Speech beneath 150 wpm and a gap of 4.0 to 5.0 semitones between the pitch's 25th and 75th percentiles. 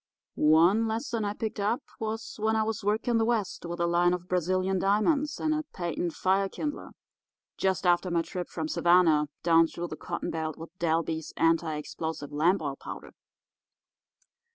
No: average, 170 wpm; average, 4.7 semitones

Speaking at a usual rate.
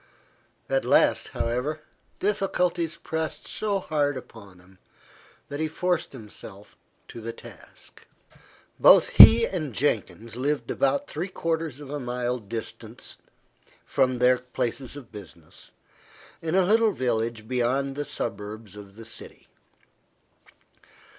No: slow, 120 wpm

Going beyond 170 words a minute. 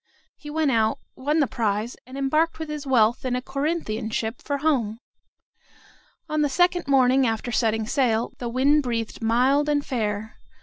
No: average, 165 wpm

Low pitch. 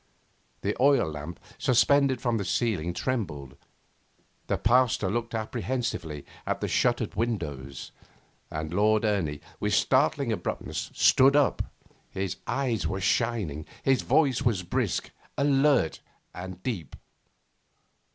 Yes: low, 110 Hz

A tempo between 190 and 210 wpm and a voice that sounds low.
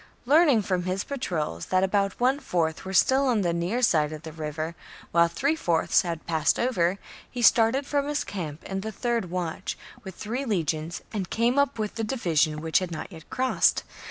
No: average, 195 wpm; high, 190 Hz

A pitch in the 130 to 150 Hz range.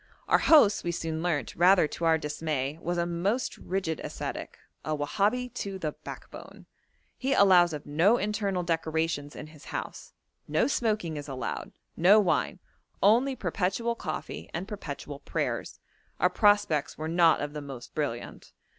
No: medium, 170 Hz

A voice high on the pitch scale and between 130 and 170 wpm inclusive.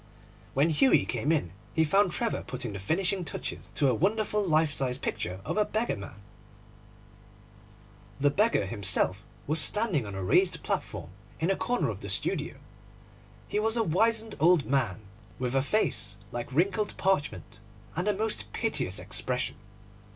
No: medium, 155 Hz; average, 160 wpm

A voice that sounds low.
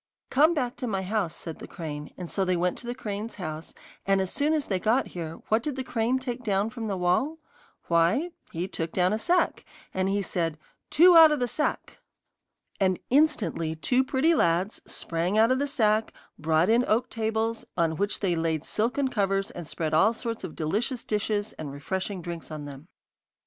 No: high, 205 Hz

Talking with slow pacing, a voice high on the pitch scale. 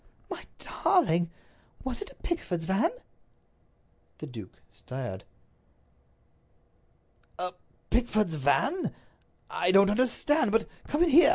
Yes: slow, 105 wpm; high, 210 Hz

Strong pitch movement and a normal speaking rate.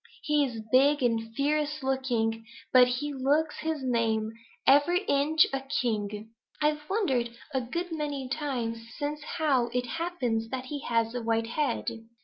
No: average, 4.2 semitones; average, 150 wpm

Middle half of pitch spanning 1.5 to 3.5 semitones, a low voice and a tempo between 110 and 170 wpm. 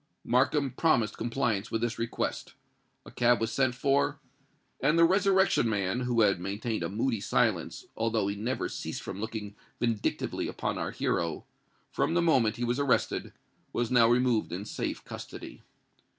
Yes: average, 3.2 semitones; low, 115 Hz; average, 160 wpm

